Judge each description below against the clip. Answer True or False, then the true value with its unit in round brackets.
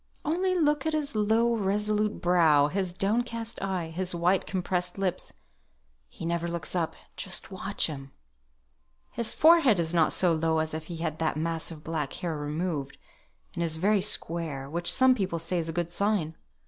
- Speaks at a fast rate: False (175 wpm)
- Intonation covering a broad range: False (4.4 semitones)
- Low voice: False (175 Hz)